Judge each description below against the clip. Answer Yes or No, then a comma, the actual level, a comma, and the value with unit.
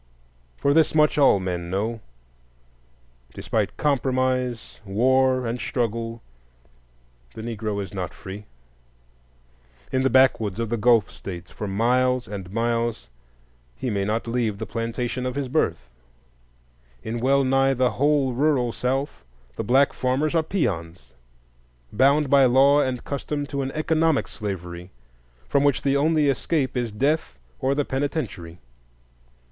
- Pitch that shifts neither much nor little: Yes, average, 4.3 semitones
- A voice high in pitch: No, low, 125 Hz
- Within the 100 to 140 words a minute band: Yes, slow, 135 wpm